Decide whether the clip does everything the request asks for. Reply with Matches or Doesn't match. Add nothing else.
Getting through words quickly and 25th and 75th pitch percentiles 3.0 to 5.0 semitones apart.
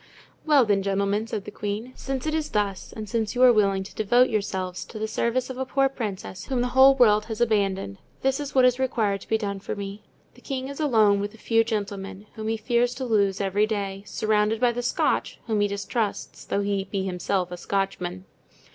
Matches